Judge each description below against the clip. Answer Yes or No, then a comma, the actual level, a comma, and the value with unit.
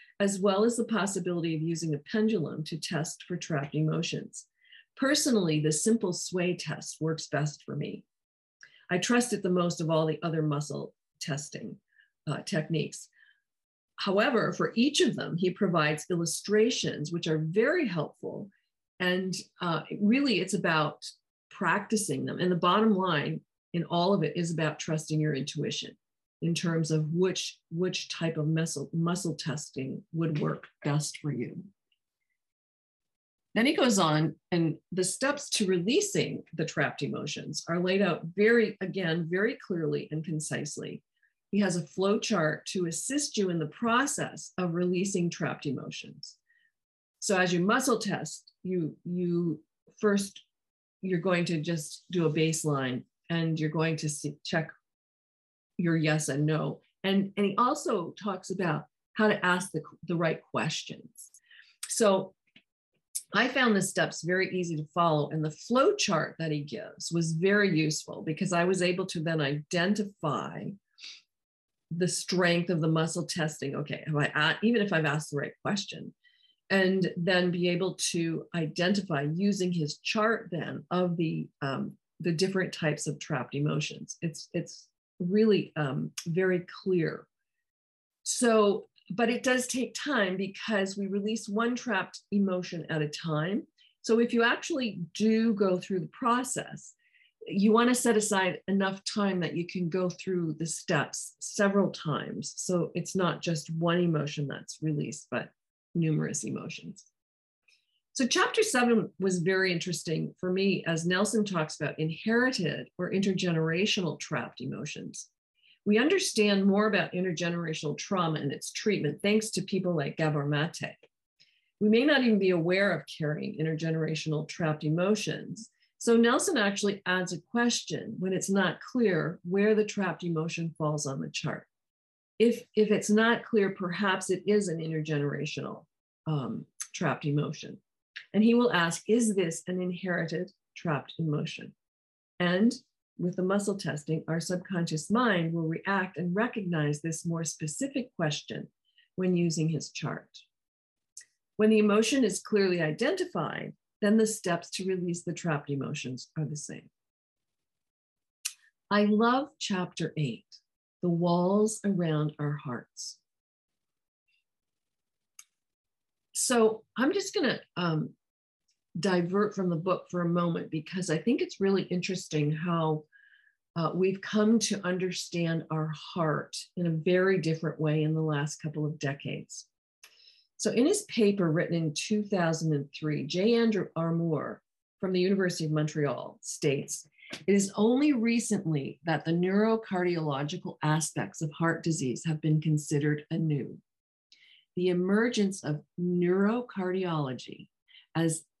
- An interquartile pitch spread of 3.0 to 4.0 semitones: No, average, 4.4 semitones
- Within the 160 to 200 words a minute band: No, average, 145 wpm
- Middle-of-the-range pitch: Yes, medium, 180 Hz